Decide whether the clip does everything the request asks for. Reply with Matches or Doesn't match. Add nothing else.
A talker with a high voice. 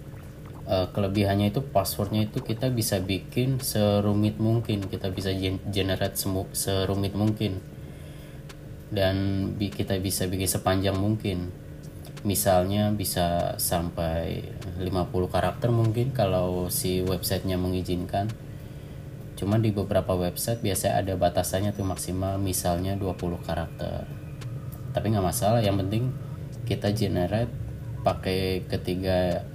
Doesn't match